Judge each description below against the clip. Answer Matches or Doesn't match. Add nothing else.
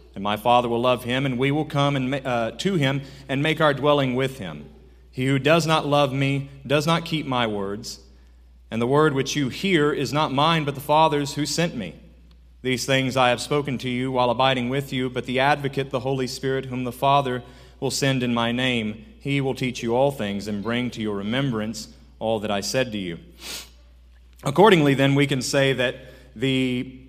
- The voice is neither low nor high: Doesn't match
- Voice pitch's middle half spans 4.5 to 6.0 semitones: Doesn't match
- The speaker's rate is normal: Doesn't match